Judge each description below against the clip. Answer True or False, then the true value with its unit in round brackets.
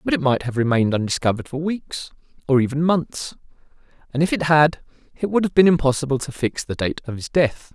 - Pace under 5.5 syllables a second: False (6.0 syllables/s)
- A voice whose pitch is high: False (140 Hz)